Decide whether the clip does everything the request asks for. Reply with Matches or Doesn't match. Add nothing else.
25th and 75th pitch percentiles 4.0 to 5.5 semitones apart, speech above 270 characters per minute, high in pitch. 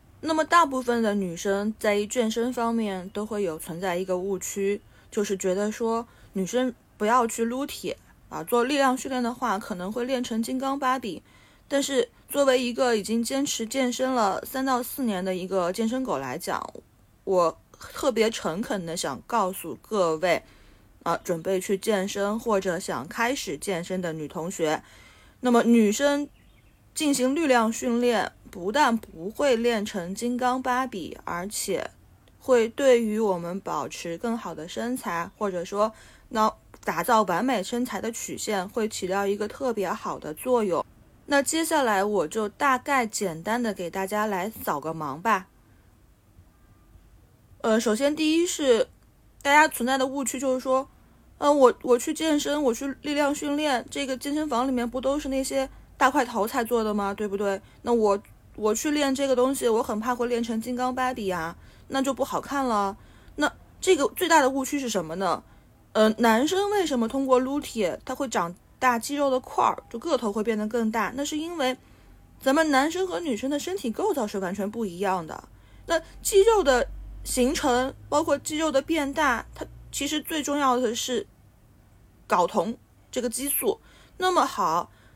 Doesn't match